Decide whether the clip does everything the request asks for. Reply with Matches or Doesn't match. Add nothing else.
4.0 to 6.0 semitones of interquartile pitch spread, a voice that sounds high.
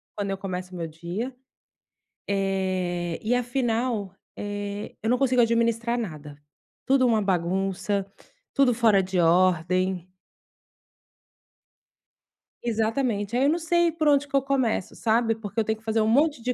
Matches